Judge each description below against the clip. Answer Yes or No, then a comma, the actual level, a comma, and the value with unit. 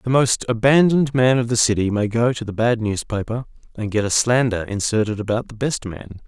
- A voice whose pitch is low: Yes, low, 115 Hz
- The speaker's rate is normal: No, fast, 210 wpm